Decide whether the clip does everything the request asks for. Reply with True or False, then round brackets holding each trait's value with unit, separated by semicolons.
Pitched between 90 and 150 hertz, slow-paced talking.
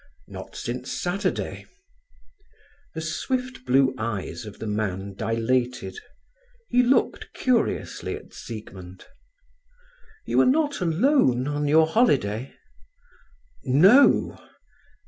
True (135 Hz; 95 wpm)